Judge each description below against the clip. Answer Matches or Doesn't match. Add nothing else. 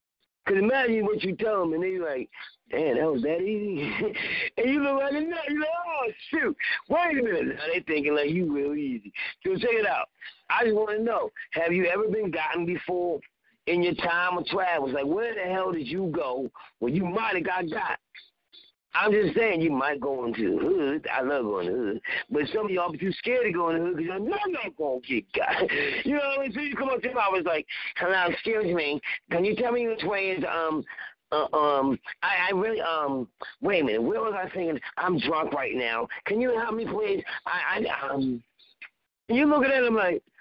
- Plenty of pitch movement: Matches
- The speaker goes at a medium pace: Doesn't match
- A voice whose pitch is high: Matches